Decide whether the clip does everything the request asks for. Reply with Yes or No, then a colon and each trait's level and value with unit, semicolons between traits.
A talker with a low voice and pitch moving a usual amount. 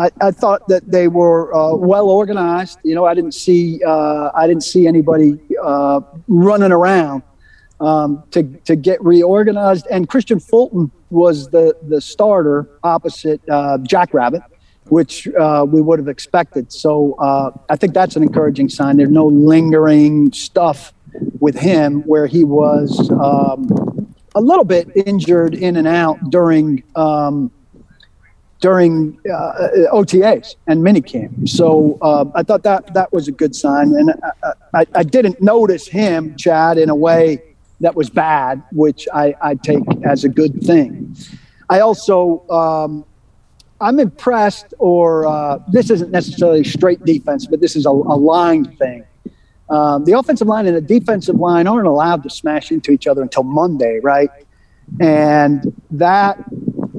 No: medium, 165 Hz; average, 3.9 semitones